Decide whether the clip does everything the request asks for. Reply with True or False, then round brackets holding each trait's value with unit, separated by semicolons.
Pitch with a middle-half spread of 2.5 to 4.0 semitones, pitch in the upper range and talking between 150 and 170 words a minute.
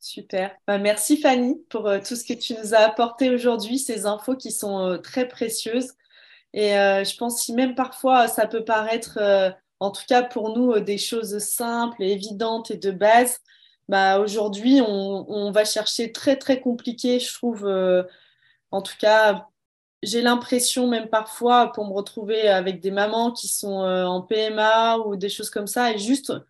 False (3.2 semitones; 220 Hz; 185 wpm)